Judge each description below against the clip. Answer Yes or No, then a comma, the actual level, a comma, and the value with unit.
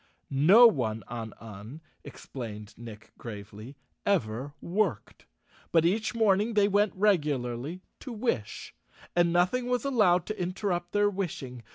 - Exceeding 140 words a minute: No, slow, 135 wpm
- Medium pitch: Yes, medium, 175 Hz